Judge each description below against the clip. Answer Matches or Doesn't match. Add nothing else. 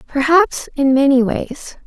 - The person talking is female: Matches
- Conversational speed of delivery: Doesn't match